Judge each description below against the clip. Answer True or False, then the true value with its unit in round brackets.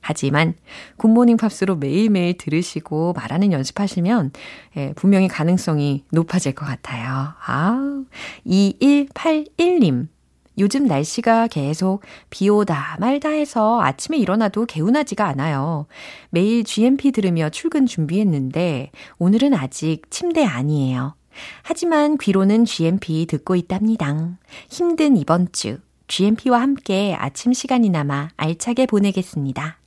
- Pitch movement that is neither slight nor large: False (7.3 semitones)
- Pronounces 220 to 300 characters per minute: True (280 characters per minute)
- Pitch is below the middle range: False (190 Hz)